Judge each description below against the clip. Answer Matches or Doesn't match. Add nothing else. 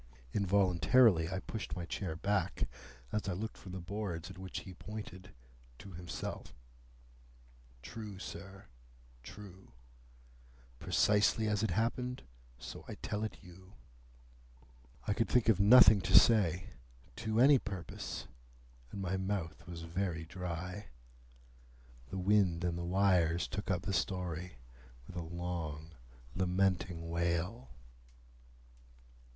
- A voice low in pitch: Matches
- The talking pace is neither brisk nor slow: Doesn't match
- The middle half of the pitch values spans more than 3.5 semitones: Doesn't match